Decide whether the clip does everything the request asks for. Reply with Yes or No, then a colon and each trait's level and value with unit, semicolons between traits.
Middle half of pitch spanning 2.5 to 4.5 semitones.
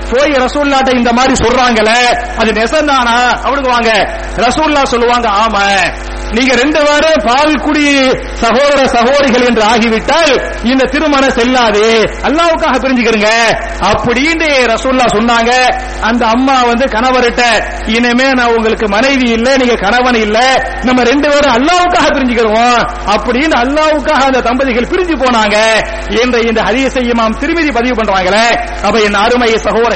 Yes: average, 3.0 semitones